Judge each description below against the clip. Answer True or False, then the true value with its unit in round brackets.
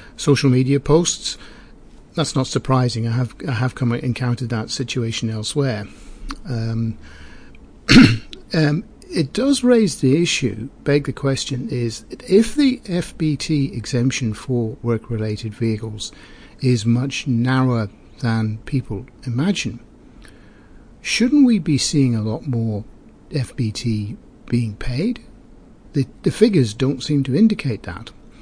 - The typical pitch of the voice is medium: False (125 Hz)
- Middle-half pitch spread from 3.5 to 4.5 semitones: True (4.2 semitones)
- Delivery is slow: True (120 wpm)